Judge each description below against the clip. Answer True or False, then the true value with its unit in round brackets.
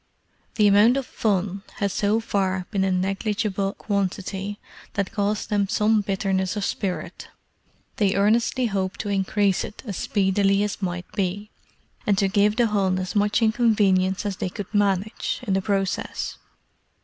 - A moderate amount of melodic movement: False (1.5 semitones)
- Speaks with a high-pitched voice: True (200 Hz)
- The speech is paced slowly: False (155 wpm)